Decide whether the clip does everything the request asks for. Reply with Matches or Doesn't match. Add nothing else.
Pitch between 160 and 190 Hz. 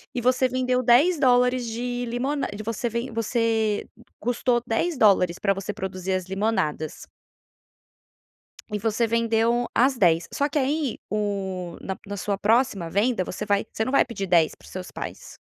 Doesn't match